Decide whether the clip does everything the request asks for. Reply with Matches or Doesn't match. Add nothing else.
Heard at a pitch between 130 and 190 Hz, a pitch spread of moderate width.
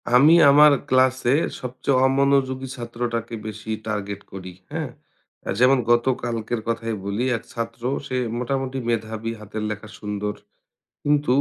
Doesn't match